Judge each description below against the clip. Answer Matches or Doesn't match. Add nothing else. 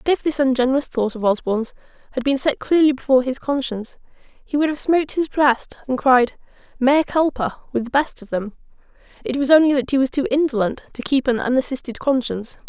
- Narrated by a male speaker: Doesn't match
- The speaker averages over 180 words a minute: Matches